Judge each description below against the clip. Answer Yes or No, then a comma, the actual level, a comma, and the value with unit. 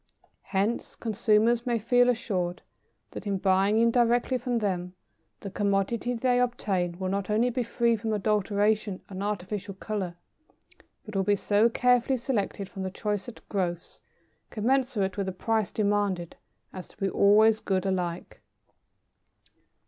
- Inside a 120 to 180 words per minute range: Yes, average, 140 wpm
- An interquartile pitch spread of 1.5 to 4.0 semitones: Yes, average, 3.3 semitones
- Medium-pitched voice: No, high, 210 Hz